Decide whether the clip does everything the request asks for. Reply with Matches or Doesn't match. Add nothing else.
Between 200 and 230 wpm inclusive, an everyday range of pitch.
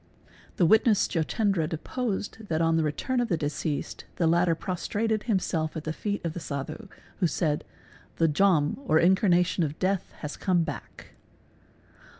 Doesn't match